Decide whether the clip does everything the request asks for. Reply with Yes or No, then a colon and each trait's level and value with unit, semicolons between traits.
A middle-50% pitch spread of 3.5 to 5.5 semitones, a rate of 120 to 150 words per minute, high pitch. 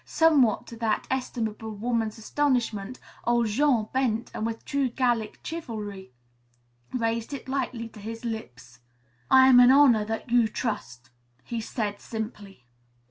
No: average, 2.8 semitones; slow, 135 wpm; high, 230 Hz